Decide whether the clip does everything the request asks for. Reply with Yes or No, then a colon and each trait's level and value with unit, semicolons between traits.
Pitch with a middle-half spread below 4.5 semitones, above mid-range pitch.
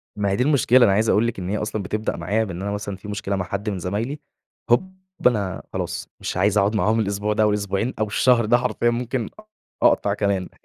No: narrow, 2.4 semitones; low, 105 Hz